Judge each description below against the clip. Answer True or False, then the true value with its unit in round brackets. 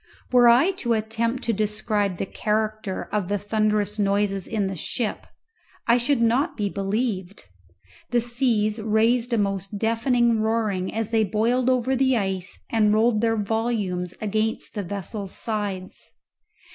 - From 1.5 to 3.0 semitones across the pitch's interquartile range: True (2.5 semitones)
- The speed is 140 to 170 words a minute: True (145 wpm)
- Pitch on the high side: True (215 Hz)